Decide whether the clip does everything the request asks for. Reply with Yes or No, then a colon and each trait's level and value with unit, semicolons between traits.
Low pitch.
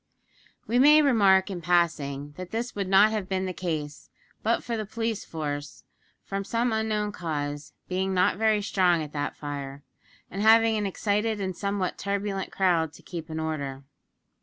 No: high, 190 Hz